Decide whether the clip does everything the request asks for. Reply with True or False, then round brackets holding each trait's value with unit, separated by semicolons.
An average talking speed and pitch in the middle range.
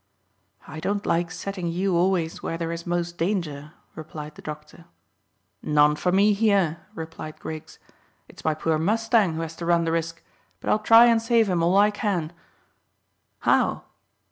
True (170 wpm; 170 Hz)